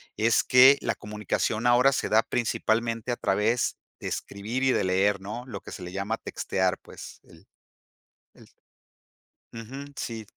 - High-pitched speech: No, low, 110 Hz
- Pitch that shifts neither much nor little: Yes, average, 3.3 semitones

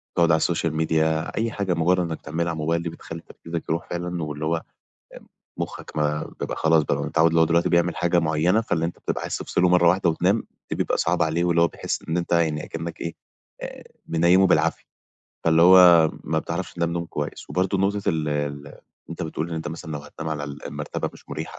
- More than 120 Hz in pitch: No, very low, 85 Hz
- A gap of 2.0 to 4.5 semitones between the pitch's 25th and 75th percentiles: No, narrow, 1.6 semitones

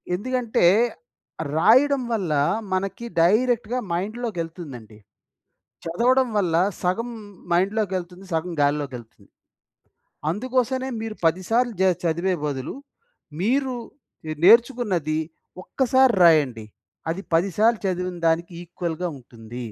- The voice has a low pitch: No, medium, 185 Hz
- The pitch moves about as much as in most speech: No, wide, 6.3 semitones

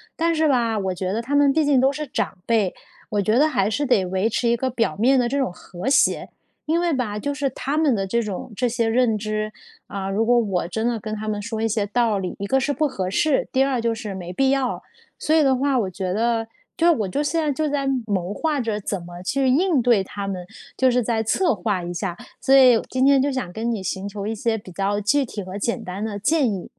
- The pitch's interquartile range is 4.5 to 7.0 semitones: Yes, average, 5.1 semitones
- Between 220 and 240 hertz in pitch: Yes, high, 230 Hz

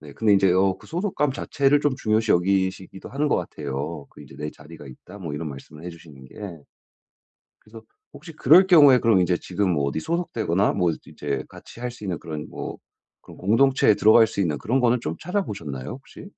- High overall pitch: No, very low, 95 Hz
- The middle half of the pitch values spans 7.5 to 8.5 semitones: Yes, wide, 8.1 semitones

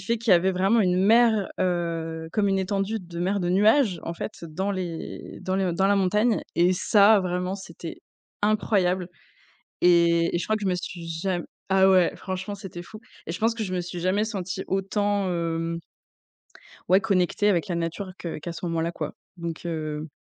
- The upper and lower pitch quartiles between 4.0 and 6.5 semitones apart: No, average, 2.8 semitones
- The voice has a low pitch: No, medium, 185 Hz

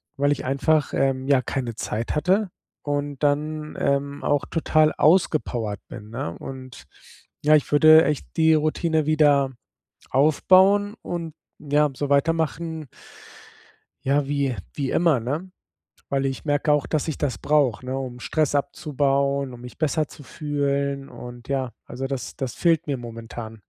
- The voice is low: No, medium, 145 Hz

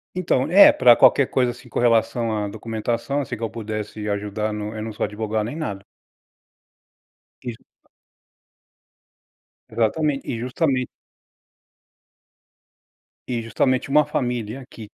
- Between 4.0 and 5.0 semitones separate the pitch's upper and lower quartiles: No, average, 3.2 semitones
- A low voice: Yes, low, 115 Hz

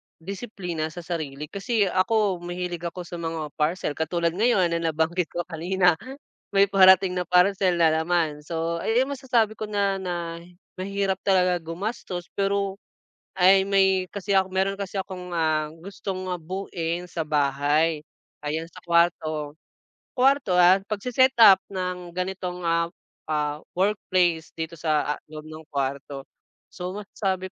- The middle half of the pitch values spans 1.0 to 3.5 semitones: Yes, average, 3.0 semitones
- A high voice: No, medium, 180 Hz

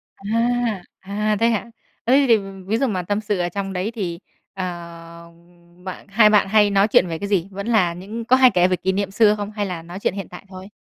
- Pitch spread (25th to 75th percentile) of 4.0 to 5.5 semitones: No, average, 2.9 semitones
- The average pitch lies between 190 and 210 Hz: Yes, high, 200 Hz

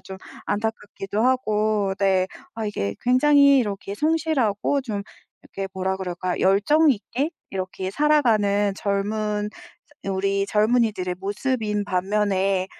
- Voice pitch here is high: Yes, high, 205 Hz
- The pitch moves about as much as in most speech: Yes, average, 3.6 semitones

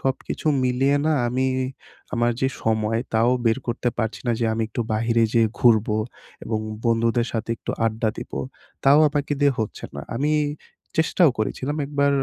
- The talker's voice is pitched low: Yes, low, 120 Hz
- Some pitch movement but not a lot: Yes, average, 3.3 semitones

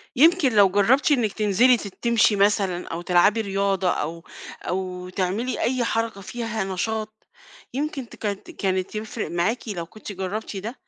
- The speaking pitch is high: Yes, high, 210 Hz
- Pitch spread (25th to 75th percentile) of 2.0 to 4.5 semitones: Yes, average, 3.6 semitones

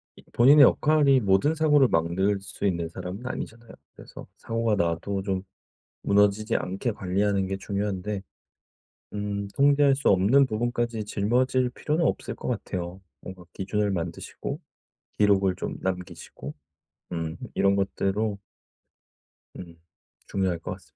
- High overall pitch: No, low, 100 Hz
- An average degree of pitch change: Yes, average, 4.0 semitones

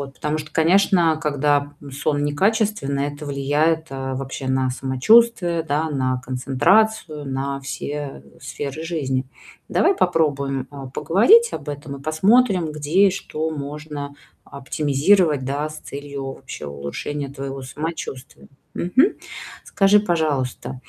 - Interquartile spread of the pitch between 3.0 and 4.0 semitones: Yes, average, 3.3 semitones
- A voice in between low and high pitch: Yes, medium, 145 Hz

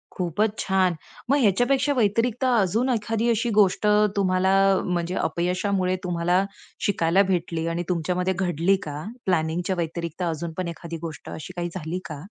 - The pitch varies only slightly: No, average, 3.3 semitones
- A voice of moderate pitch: Yes, medium, 180 Hz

